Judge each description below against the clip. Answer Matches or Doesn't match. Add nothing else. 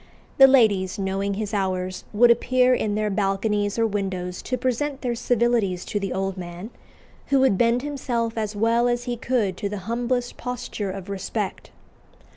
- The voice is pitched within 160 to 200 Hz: Doesn't match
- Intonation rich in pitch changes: Doesn't match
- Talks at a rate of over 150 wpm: Matches